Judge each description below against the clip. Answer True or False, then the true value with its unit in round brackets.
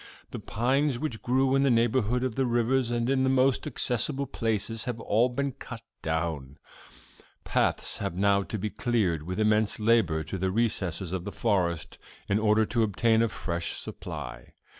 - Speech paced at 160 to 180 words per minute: True (175 wpm)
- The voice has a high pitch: False (115 Hz)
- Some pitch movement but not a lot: True (4.4 semitones)